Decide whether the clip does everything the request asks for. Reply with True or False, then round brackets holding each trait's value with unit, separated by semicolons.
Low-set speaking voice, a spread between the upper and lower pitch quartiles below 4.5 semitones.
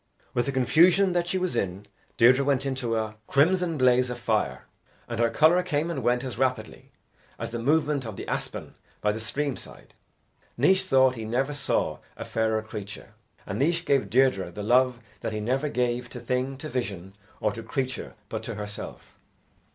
True (125 Hz; 4.1 semitones)